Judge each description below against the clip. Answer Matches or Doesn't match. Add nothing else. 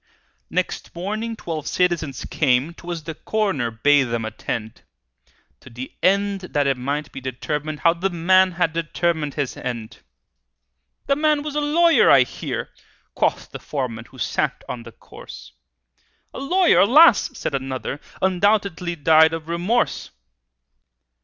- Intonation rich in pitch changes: Matches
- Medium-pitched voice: Matches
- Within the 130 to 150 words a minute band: Matches